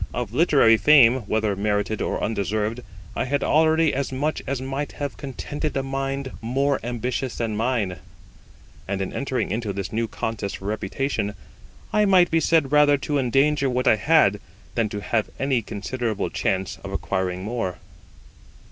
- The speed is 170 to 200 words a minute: No, average, 160 wpm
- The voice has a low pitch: Yes, low, 125 Hz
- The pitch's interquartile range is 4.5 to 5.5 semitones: Yes, average, 4.8 semitones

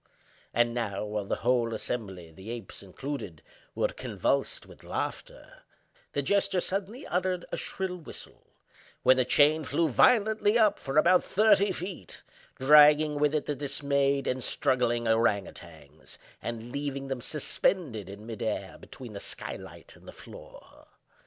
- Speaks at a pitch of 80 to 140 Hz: Yes, low, 135 Hz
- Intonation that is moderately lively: No, wide, 6.5 semitones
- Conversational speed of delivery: Yes, average, 145 wpm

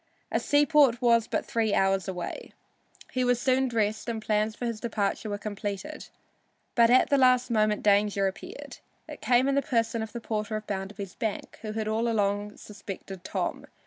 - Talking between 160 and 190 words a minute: Yes, average, 180 wpm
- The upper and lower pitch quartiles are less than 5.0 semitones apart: Yes, average, 2.8 semitones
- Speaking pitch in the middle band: No, high, 220 Hz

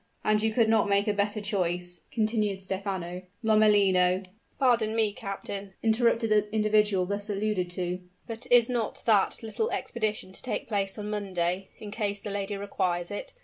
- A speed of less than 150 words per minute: No, average, 170 wpm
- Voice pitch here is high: Yes, high, 205 Hz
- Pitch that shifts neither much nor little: No, narrow, 2.2 semitones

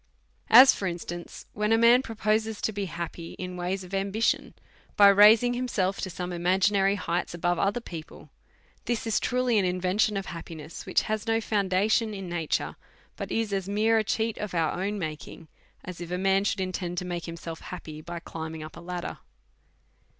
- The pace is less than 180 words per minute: No, average, 195 wpm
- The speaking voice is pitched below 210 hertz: Yes, high, 190 Hz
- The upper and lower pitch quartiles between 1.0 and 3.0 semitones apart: No, average, 3.5 semitones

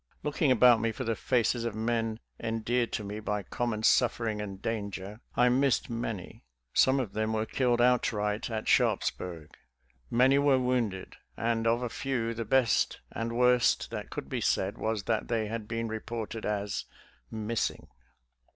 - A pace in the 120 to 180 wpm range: Yes, average, 165 wpm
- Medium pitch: No, low, 115 Hz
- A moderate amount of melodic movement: No, narrow, 2.2 semitones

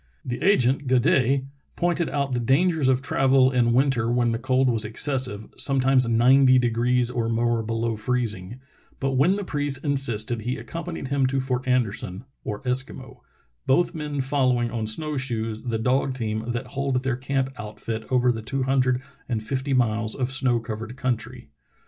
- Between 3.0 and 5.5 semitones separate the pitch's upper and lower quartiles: No, narrow, 2.5 semitones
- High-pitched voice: No, low, 125 Hz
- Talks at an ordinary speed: Yes, average, 170 wpm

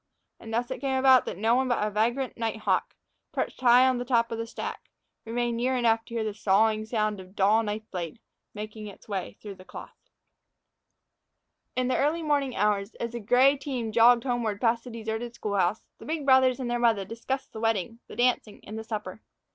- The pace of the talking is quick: Yes, fast, 210 wpm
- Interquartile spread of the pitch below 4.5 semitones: Yes, narrow, 2.6 semitones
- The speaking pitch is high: Yes, high, 230 Hz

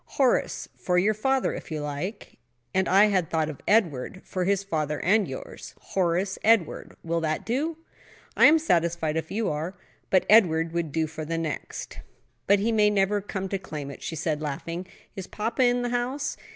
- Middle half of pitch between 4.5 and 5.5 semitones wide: Yes, average, 4.9 semitones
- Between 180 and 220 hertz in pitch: Yes, medium, 185 Hz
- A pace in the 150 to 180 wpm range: No, average, 190 wpm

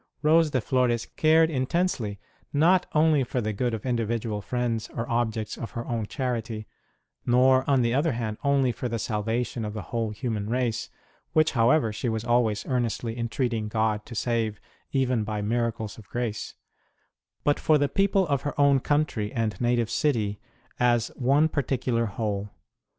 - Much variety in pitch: No, average, 3.3 semitones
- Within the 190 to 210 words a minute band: No, average, 165 wpm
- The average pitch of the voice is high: No, low, 120 Hz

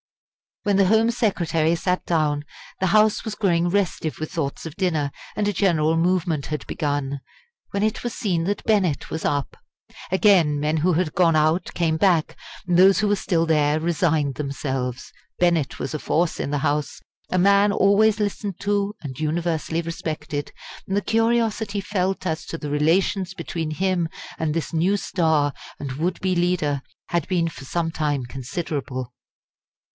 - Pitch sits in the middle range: Yes, medium, 170 Hz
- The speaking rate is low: No, average, 170 wpm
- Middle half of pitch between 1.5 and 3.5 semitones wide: No, average, 4.2 semitones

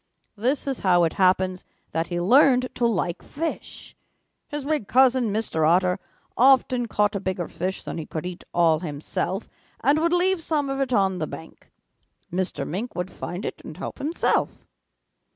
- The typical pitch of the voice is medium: No, high, 200 Hz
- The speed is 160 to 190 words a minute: Yes, average, 170 wpm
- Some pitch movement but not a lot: No, wide, 6.9 semitones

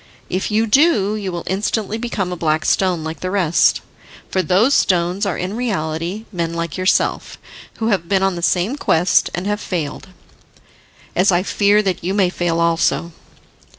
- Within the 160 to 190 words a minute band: Yes, average, 175 wpm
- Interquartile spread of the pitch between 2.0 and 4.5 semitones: Yes, average, 3.2 semitones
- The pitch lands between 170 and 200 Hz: Yes, medium, 185 Hz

